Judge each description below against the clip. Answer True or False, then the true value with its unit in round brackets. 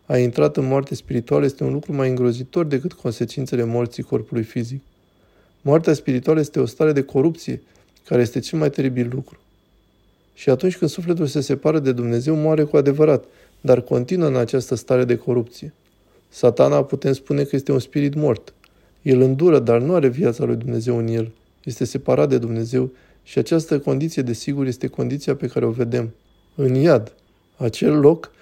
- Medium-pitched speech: False (130 Hz)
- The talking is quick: True (175 wpm)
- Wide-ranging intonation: False (3.4 semitones)